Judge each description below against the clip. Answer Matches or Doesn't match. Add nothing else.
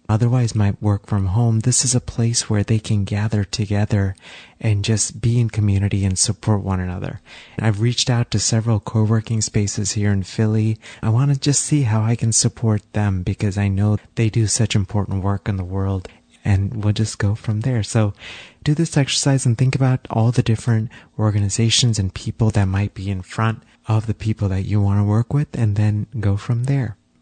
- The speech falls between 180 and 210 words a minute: Matches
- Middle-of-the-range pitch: Doesn't match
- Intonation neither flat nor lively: Doesn't match